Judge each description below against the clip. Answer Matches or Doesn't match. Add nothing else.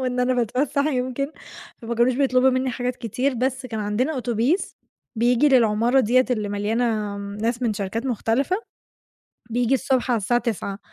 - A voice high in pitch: Matches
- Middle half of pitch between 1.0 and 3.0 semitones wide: Matches